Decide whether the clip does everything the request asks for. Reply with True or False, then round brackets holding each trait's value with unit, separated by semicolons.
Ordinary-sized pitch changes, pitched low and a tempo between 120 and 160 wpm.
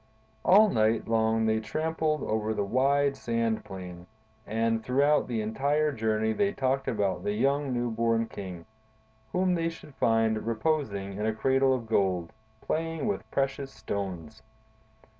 True (4.4 semitones; 115 Hz; 145 wpm)